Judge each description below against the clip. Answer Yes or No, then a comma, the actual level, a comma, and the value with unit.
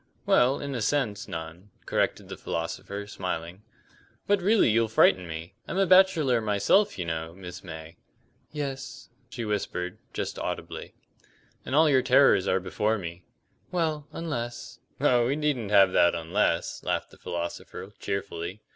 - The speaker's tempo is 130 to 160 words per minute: Yes, average, 150 wpm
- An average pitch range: No, wide, 7.9 semitones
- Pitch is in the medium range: No, low, 105 Hz